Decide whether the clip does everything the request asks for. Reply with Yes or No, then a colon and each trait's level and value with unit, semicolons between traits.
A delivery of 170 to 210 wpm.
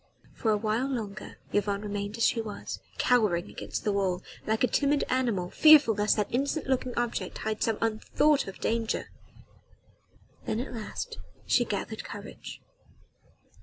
No: average, 150 wpm